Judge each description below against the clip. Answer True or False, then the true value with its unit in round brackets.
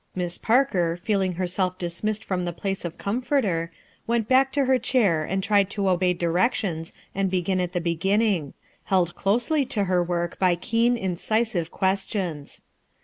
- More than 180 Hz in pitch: True (190 Hz)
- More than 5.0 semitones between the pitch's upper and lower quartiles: False (3.7 semitones)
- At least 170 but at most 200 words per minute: False (160 wpm)